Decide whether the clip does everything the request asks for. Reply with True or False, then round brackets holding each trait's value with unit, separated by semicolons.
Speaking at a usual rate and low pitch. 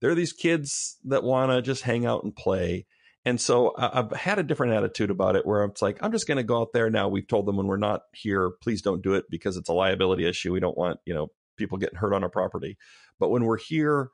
False (265 wpm; 115 Hz)